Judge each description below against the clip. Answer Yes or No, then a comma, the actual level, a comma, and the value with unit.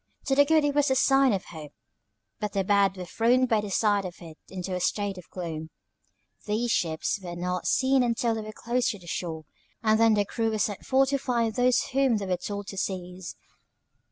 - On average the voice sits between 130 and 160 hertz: No, high, 210 Hz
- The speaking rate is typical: No, fast, 220 wpm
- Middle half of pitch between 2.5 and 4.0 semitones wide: No, average, 5.1 semitones